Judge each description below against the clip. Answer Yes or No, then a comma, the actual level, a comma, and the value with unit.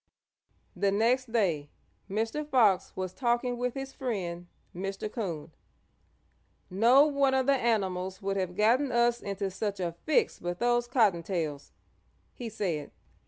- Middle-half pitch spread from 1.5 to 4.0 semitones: No, average, 4.8 semitones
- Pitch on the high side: Yes, high, 210 Hz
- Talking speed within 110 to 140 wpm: Yes, slow, 135 wpm